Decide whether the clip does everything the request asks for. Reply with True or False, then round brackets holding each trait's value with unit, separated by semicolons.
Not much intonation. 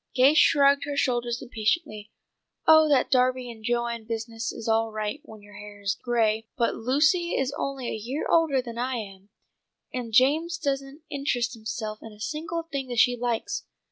False (3.9 semitones)